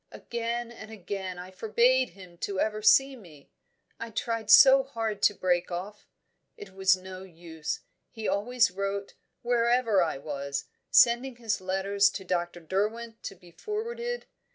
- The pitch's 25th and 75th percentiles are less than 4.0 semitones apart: No, average, 4.3 semitones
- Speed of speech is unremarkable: Yes, average, 150 wpm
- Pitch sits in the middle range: No, high, 205 Hz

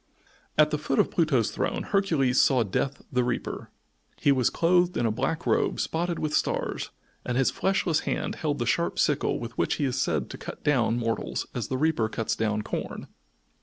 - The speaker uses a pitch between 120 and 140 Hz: Yes, low, 135 Hz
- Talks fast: No, average, 195 wpm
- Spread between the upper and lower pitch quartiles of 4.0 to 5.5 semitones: Yes, average, 5.0 semitones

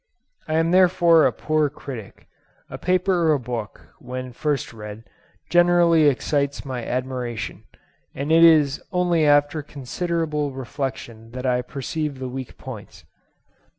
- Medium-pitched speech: Yes, medium, 145 Hz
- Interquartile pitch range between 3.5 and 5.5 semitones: Yes, average, 4.4 semitones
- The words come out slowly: Yes, slow, 130 wpm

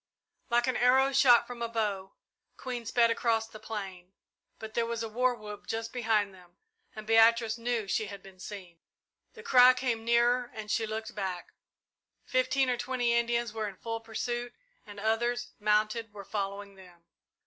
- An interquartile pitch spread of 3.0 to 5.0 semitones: No, narrow, 2.5 semitones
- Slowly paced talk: No, average, 170 wpm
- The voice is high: Yes, high, 225 Hz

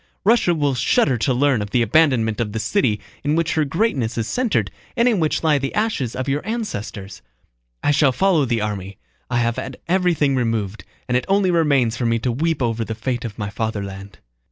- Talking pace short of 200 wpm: No, fast, 205 wpm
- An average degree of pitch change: No, wide, 6.2 semitones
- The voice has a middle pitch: No, low, 130 Hz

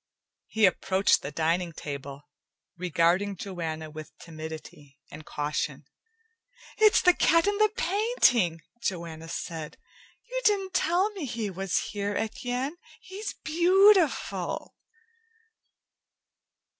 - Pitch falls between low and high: No, high, 195 Hz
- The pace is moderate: No, slow, 105 wpm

